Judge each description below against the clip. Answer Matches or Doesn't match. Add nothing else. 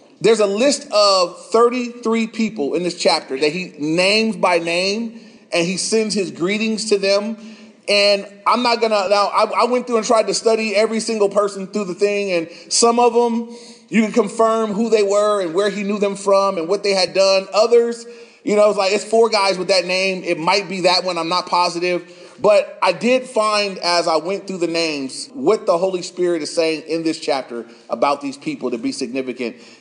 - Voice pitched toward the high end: Matches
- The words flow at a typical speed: Doesn't match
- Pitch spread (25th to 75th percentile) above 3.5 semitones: Matches